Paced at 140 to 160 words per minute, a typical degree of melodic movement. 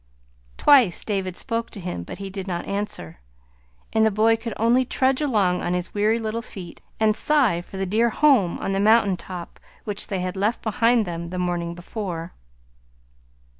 No: average, 180 wpm; average, 4.0 semitones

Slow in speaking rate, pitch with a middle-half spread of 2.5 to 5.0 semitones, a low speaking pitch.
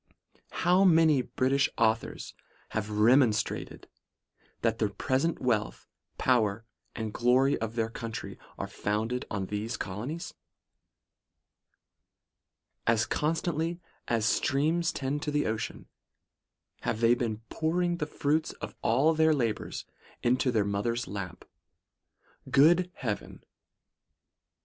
No: slow, 110 wpm; wide, 5.6 semitones; low, 125 Hz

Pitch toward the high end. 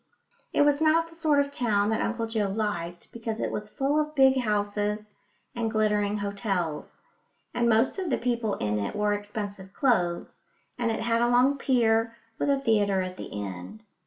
Yes: high, 220 Hz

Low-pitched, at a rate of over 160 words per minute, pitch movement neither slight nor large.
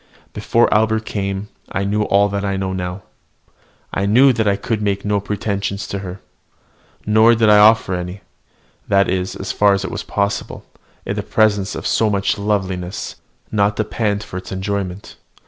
No: low, 100 Hz; average, 175 wpm; narrow, 1.6 semitones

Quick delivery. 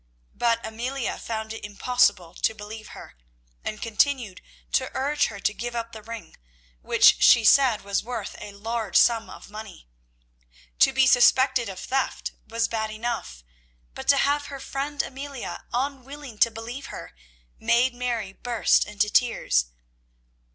No: average, 150 wpm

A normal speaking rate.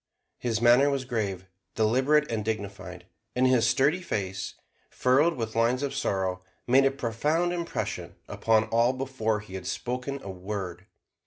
Yes: average, 150 wpm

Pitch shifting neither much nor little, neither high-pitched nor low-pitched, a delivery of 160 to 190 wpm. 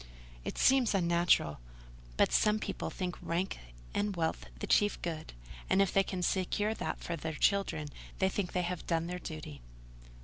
Yes: average, 3.1 semitones; medium, 180 Hz; average, 170 wpm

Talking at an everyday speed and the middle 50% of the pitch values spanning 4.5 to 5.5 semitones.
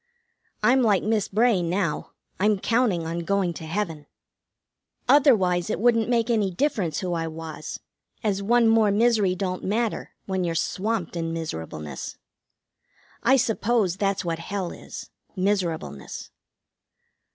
No: slow, 130 wpm; average, 4.8 semitones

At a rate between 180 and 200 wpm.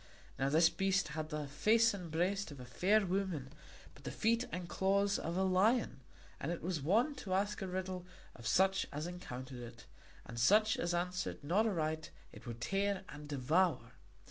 Yes: average, 185 wpm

